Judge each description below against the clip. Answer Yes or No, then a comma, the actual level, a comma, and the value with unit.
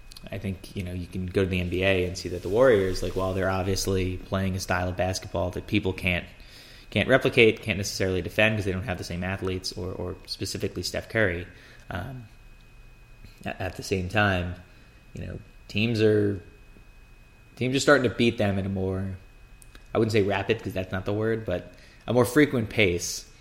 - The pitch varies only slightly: No, average, 3.2 semitones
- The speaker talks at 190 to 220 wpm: Yes, average, 195 wpm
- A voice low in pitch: Yes, very low, 95 Hz